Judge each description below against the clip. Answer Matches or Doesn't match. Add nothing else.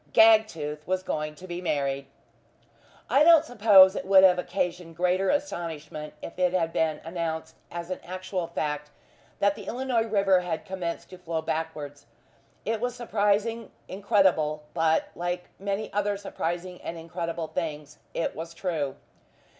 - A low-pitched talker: Doesn't match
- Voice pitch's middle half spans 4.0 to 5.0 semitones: Doesn't match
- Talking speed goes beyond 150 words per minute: Doesn't match